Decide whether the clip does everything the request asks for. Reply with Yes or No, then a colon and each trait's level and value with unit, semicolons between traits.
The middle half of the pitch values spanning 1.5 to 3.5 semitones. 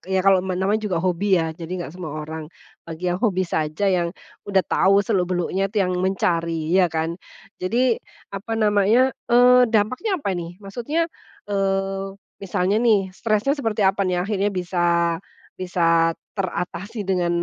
Yes: average, 2.7 semitones